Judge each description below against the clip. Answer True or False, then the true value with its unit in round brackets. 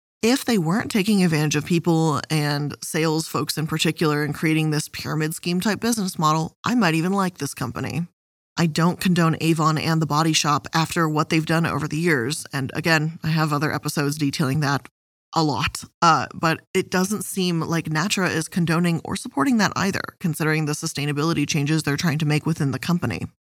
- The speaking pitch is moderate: True (160 Hz)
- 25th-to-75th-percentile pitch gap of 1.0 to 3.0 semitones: True (2.4 semitones)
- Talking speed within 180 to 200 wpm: True (190 wpm)